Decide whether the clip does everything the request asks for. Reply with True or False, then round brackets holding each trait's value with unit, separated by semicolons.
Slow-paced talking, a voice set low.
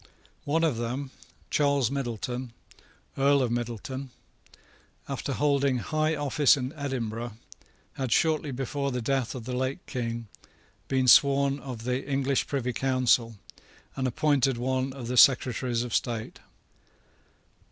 True (130 wpm; 130 Hz)